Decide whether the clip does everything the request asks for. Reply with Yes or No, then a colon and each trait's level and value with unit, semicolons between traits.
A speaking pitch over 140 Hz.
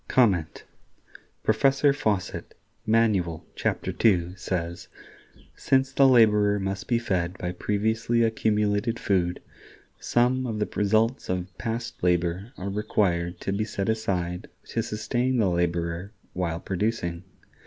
No: low, 105 Hz